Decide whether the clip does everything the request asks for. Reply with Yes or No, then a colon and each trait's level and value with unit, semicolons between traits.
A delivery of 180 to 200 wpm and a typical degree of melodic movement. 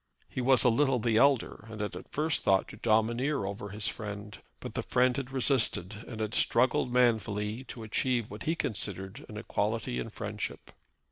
Yes: average, 185 wpm; average, 3.3 semitones